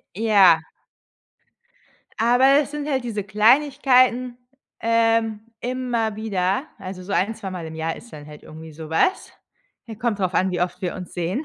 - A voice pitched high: Yes, high, 215 Hz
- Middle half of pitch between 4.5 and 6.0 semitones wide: Yes, average, 5.2 semitones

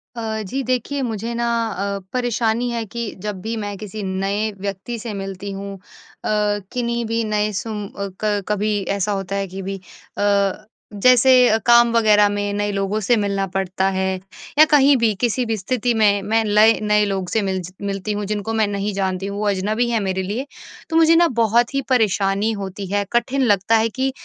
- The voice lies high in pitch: Yes, high, 210 Hz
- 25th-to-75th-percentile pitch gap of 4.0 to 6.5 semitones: No, average, 2.8 semitones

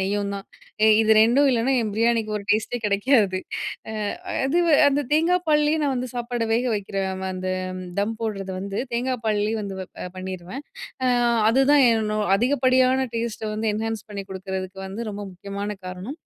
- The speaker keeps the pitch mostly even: No, average, 4.3 semitones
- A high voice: Yes, high, 220 Hz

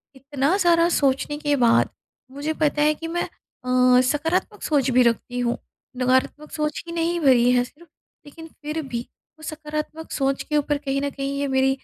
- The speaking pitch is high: Yes, very high, 285 Hz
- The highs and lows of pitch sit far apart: No, average, 3.0 semitones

